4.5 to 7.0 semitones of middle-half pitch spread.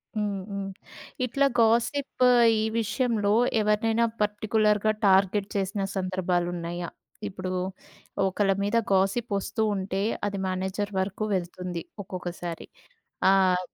No: narrow, 2.4 semitones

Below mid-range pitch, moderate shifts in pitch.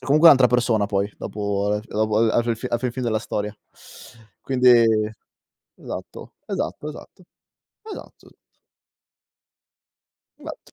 Yes: low, 115 Hz; average, 3.0 semitones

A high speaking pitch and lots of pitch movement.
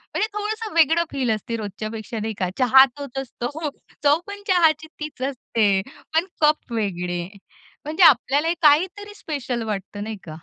Yes: very high, 280 Hz; wide, 6.7 semitones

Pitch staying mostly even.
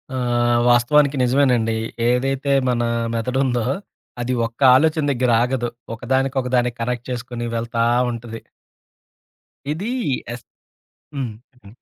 Yes: narrow, 2.0 semitones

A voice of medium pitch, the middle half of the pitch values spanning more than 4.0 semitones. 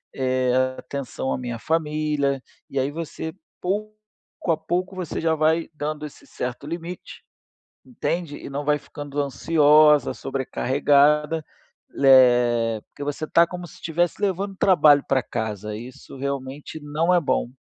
No: medium, 150 Hz; average, 3.6 semitones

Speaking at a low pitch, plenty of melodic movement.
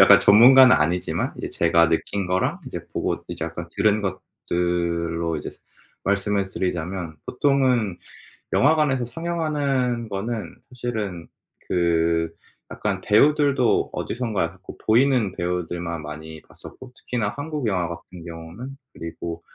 Yes: low, 100 Hz; wide, 6.7 semitones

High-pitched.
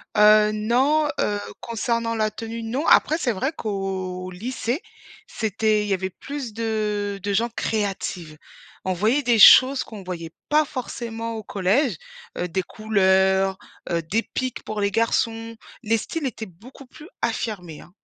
Yes: high, 215 Hz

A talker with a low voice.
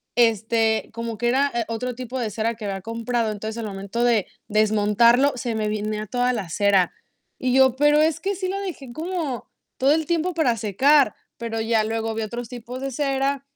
No: high, 235 Hz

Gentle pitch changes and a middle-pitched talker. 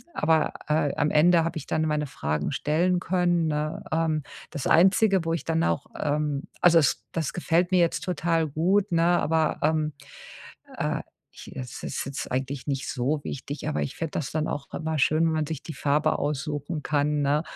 Yes: narrow, 2.2 semitones; medium, 155 Hz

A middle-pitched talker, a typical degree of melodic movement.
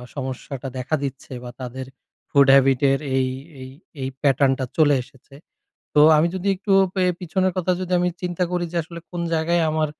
Yes: medium, 150 Hz; average, 4.7 semitones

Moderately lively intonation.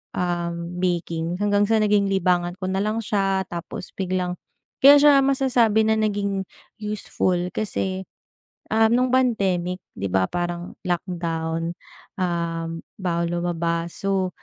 Yes: average, 3.2 semitones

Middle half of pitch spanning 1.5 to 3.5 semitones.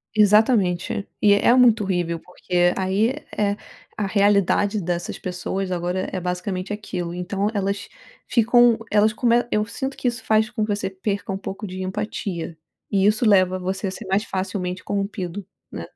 Yes: narrow, 2.5 semitones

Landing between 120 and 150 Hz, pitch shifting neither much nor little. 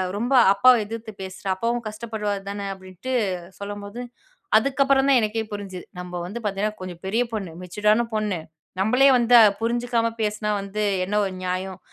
No: high, 210 Hz; average, 3.2 semitones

